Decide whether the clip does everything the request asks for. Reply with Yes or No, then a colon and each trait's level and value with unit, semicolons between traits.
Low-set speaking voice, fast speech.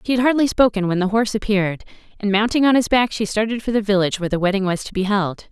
No: high, 210 Hz; fast, 270 wpm